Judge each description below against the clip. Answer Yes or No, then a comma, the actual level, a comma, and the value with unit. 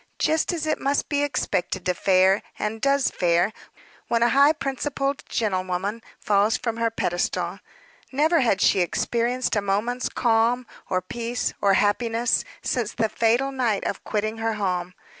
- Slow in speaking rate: No, average, 155 wpm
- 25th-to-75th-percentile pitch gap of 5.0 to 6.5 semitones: No, average, 4.3 semitones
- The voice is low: No, high, 230 Hz